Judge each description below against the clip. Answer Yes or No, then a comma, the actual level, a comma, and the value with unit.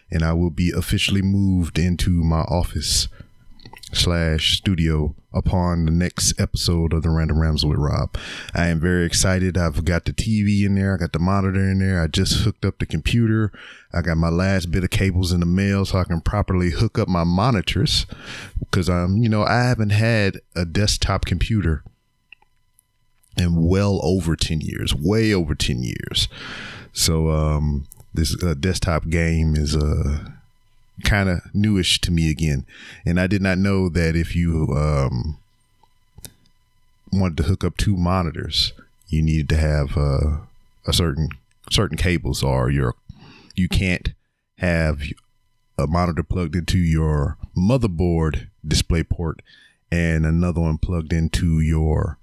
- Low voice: Yes, very low, 90 Hz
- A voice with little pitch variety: No, average, 3.4 semitones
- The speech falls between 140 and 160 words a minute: Yes, average, 155 wpm